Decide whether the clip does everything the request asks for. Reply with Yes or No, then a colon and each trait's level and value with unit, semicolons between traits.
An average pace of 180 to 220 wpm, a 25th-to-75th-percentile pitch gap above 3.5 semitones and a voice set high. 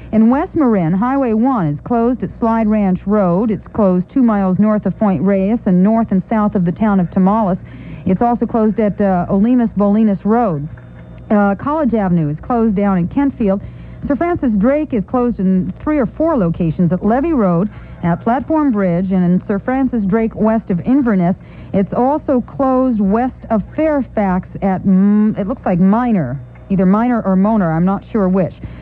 Yes: average, 185 wpm; average, 4.0 semitones; high, 210 Hz